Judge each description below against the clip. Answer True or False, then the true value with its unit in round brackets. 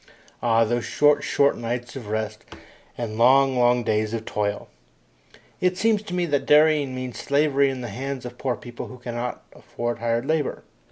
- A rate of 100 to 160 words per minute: False (175 wpm)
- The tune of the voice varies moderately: True (3.3 semitones)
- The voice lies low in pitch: True (125 Hz)